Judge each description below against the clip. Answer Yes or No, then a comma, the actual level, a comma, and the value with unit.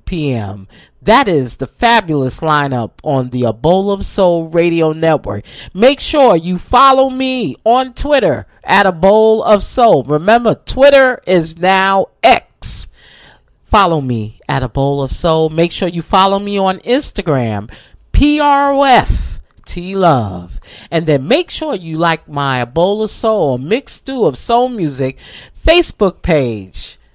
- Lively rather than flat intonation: Yes, wide, 8.4 semitones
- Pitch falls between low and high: Yes, medium, 175 Hz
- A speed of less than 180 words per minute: Yes, average, 145 wpm